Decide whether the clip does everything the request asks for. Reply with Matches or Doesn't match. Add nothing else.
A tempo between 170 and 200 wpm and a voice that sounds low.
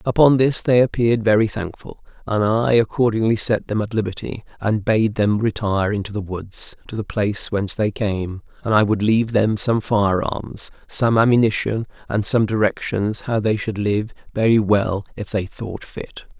Matches